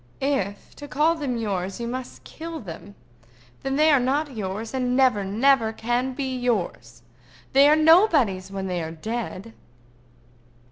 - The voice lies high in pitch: Yes, high, 240 Hz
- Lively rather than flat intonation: Yes, wide, 5.7 semitones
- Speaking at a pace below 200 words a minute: Yes, average, 150 wpm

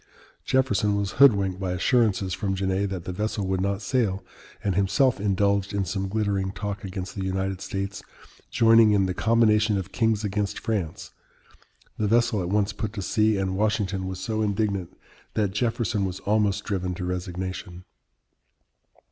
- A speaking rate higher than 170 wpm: No, average, 160 wpm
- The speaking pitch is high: No, low, 100 Hz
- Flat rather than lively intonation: Yes, narrow, 2.1 semitones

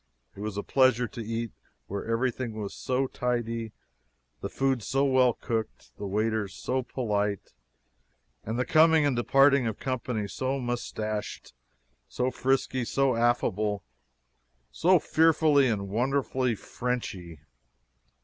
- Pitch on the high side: No, low, 120 Hz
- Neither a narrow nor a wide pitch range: Yes, average, 3.4 semitones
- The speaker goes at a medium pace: No, slow, 120 wpm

